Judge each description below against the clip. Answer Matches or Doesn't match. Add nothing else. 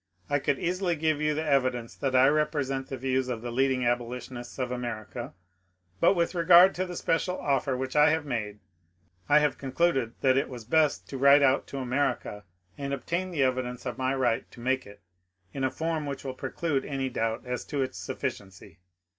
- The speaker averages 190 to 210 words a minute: Matches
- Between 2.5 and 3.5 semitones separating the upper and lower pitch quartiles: Matches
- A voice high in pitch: Doesn't match